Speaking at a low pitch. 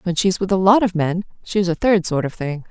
No: medium, 180 Hz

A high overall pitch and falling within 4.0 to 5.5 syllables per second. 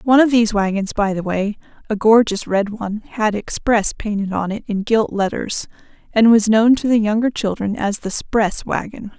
Yes: high, 215 Hz; 4.9 syllables/s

